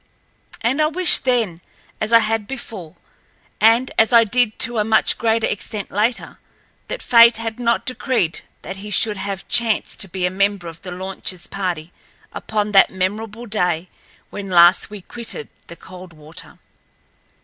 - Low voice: No, high, 210 Hz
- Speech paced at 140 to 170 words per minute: Yes, average, 160 wpm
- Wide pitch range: No, average, 3.8 semitones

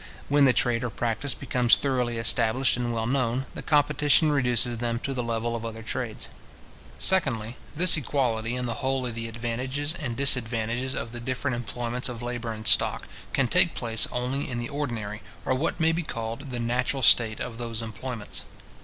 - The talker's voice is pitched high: No, low, 120 Hz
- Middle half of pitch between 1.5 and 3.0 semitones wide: Yes, average, 2.7 semitones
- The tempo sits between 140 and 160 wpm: No, average, 185 wpm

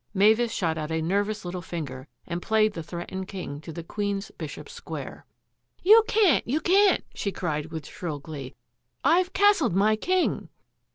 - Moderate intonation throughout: No, wide, 7.0 semitones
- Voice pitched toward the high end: Yes, high, 195 Hz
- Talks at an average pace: Yes, average, 180 wpm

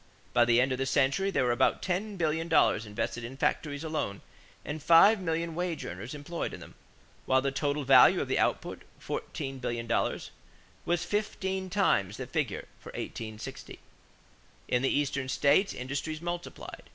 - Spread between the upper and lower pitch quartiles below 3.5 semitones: No, average, 5.1 semitones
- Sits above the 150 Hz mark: No, medium, 145 Hz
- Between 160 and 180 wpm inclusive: Yes, average, 165 wpm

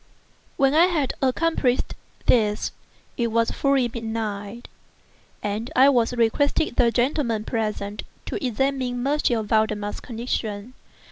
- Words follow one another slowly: Yes, slow, 110 wpm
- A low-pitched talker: No, high, 235 Hz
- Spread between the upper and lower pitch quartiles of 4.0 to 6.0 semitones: No, average, 3.6 semitones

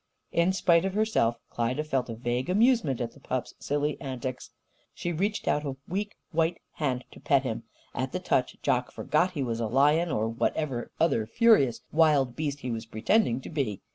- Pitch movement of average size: No, wide, 5.7 semitones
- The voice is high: No, medium, 140 Hz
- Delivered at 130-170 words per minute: No, average, 190 wpm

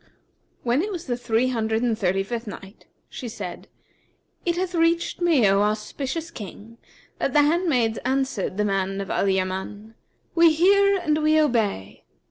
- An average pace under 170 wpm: Yes, average, 160 wpm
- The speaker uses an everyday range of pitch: No, wide, 7.3 semitones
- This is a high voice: Yes, high, 240 Hz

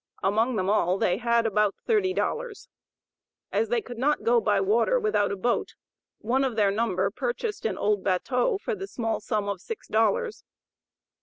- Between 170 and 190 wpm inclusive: Yes, average, 175 wpm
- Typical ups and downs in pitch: No, wide, 6.4 semitones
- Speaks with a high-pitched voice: Yes, high, 230 Hz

